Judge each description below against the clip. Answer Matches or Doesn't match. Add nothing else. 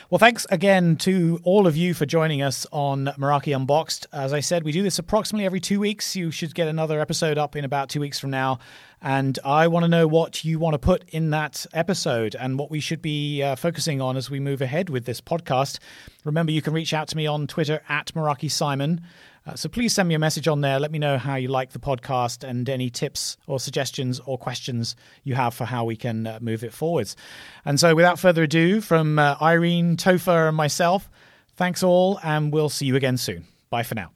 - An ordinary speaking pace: Doesn't match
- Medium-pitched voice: Matches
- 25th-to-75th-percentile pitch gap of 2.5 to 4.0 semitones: Matches